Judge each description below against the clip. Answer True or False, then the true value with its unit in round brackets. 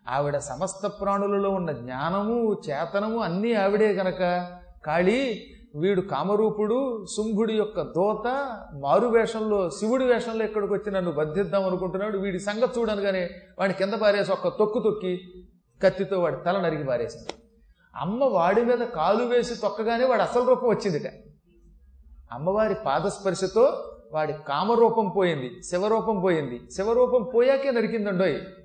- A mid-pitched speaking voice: False (200 Hz)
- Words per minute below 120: False (125 wpm)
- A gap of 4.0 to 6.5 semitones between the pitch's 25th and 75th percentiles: False (3.6 semitones)